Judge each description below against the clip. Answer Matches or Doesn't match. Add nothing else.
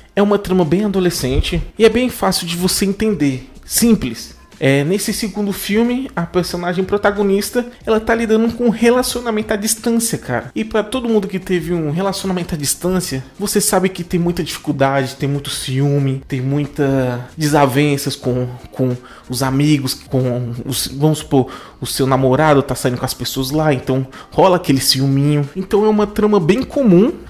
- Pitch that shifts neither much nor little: Doesn't match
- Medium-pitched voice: Matches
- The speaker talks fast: Doesn't match